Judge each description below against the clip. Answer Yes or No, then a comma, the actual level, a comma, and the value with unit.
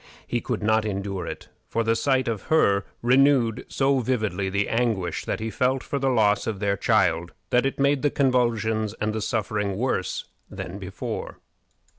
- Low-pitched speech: Yes, low, 110 Hz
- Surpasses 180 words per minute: No, average, 175 wpm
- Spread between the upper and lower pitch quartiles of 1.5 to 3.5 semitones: No, average, 4.1 semitones